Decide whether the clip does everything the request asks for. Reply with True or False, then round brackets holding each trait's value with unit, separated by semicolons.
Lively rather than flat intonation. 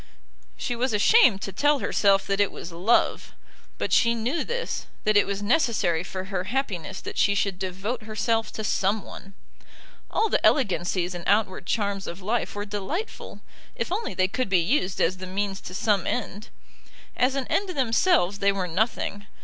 False (4.1 semitones)